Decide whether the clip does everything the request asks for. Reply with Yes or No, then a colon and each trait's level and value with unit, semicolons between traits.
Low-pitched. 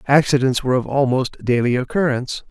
Yes: low, 130 Hz